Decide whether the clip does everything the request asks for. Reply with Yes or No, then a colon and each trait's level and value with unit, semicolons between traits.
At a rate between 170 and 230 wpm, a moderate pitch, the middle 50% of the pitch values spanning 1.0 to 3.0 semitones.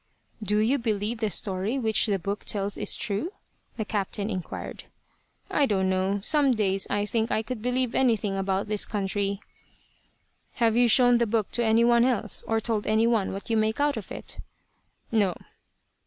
No: average, 180 wpm; high, 215 Hz; average, 2.7 semitones